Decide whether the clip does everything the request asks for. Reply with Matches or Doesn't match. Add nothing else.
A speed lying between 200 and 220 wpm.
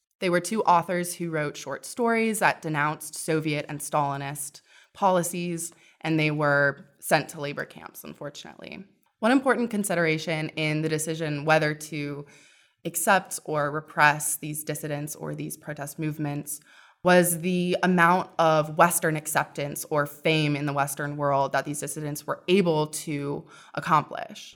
Doesn't match